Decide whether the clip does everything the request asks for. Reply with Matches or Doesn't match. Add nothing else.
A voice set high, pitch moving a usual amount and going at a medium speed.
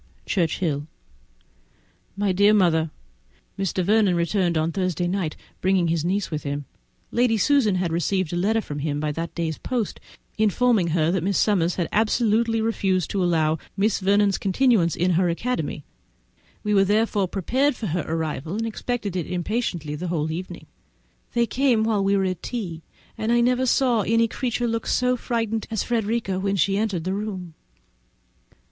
Matches